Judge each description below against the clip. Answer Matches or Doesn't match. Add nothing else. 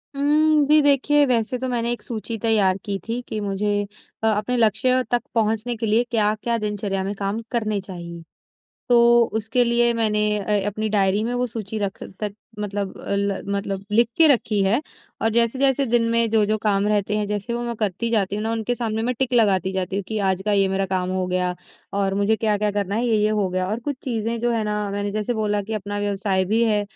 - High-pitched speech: Matches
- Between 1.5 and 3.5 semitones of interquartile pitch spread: Matches